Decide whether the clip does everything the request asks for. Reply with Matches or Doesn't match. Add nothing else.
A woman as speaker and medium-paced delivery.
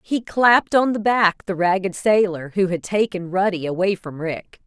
Matches